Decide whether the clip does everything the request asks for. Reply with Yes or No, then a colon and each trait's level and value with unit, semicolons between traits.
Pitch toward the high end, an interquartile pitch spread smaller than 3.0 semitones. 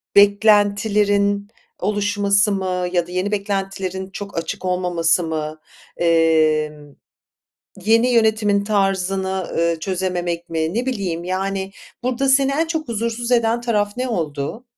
No: high, 195 Hz; average, 3.5 semitones